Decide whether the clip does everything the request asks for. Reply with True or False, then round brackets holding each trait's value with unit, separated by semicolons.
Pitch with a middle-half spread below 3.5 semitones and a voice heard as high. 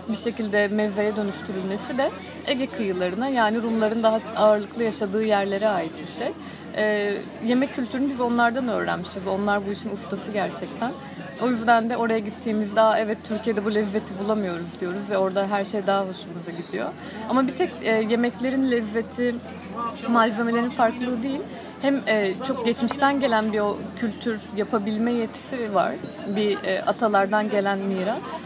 True (2.5 semitones; 220 Hz)